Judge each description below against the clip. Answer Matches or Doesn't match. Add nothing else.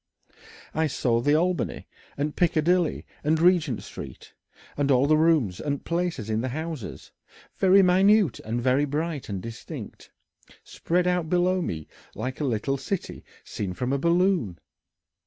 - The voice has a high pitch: Doesn't match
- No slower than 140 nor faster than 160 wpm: Matches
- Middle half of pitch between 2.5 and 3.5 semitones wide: Doesn't match